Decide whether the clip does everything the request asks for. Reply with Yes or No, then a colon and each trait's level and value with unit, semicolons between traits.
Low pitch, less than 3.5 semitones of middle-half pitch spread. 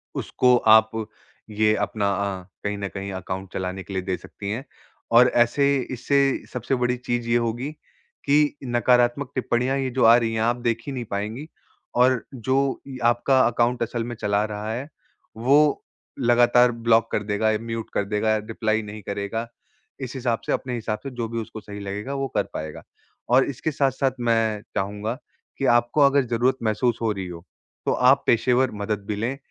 Yes: low, 115 Hz; average, 3.1 semitones